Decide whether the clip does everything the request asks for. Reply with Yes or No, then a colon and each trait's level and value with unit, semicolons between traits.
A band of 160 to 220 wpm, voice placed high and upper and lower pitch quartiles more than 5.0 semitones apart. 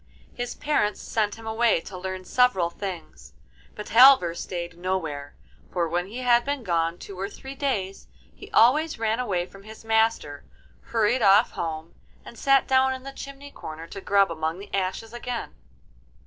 Yes: average, 170 wpm; high, 205 Hz; wide, 5.6 semitones